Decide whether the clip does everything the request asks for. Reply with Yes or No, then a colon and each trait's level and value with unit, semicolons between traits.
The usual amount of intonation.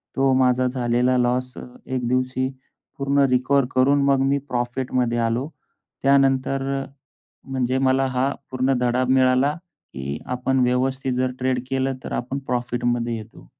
No: narrow, 1.2 semitones